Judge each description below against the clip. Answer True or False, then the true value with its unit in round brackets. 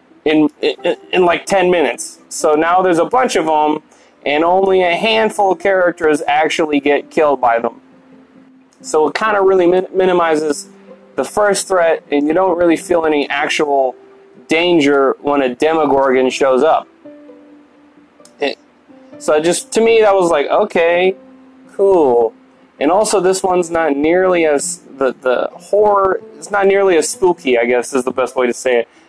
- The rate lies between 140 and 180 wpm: True (165 wpm)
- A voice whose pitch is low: False (180 Hz)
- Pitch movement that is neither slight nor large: False (5.9 semitones)